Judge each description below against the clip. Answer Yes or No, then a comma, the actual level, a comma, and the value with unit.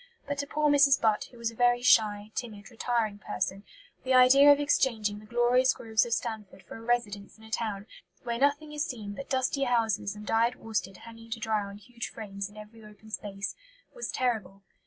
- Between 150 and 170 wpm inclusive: No, average, 200 wpm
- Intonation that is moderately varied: Yes, average, 3.2 semitones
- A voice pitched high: Yes, high, 225 Hz